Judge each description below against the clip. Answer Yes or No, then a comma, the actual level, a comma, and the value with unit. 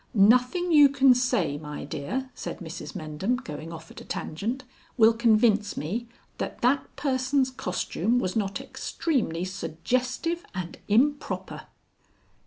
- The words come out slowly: Yes, slow, 130 wpm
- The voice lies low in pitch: No, high, 230 Hz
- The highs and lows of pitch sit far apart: Yes, wide, 7.0 semitones